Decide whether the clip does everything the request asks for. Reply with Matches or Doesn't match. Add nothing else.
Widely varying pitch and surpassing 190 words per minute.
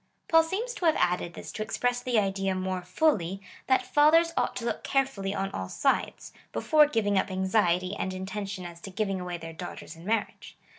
Matches